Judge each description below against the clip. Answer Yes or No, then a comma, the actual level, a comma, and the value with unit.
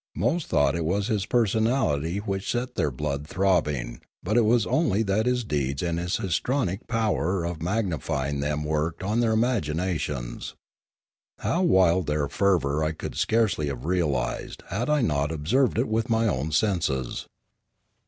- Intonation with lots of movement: Yes, wide, 6.9 semitones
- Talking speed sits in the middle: Yes, average, 165 wpm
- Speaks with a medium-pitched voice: No, very low, 90 Hz